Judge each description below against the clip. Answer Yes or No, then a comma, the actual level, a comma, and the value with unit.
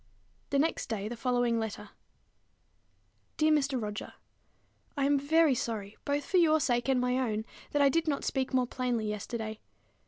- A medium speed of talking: Yes, average, 175 wpm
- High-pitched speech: Yes, very high, 255 Hz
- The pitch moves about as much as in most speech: Yes, average, 4.0 semitones